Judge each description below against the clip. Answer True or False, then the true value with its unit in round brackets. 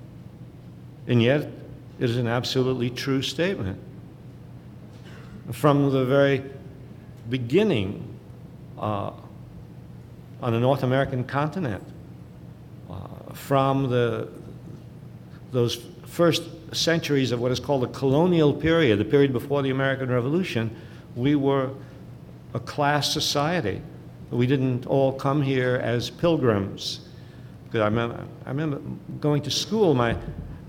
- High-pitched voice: False (135 Hz)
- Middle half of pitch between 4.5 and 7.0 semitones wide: False (3.0 semitones)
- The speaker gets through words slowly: True (105 wpm)